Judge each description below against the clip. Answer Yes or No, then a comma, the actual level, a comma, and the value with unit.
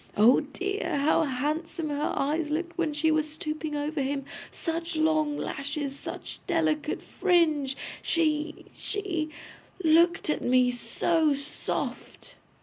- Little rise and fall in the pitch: Yes, narrow, 2.3 semitones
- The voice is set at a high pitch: Yes, very high, 310 Hz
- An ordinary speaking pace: No, slow, 125 wpm